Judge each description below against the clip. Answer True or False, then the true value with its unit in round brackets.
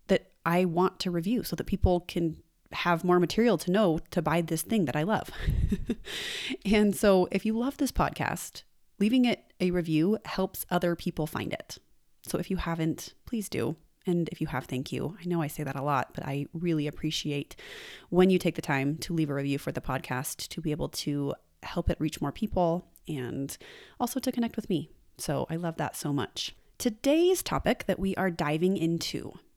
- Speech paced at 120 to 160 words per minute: False (200 wpm)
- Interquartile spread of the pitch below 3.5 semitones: False (4.3 semitones)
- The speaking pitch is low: False (170 Hz)